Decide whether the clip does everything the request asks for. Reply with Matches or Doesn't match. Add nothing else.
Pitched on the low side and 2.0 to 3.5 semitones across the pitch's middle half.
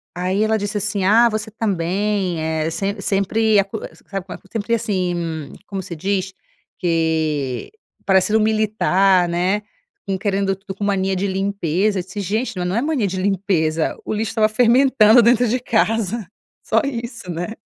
Doesn't match